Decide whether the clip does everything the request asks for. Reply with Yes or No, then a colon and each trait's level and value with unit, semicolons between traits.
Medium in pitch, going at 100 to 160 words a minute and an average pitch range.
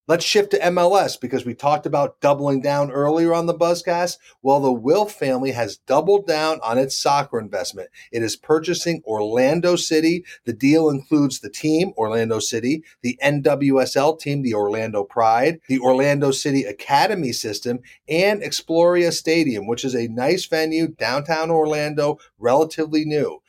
Yes: medium, 145 Hz; average, 155 wpm; average, 4.0 semitones